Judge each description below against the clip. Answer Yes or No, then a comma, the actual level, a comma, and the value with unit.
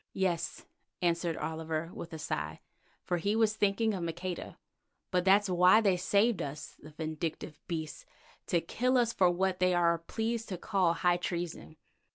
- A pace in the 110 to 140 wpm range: No, average, 165 wpm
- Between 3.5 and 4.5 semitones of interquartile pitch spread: No, average, 3.0 semitones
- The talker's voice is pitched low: No, medium, 175 Hz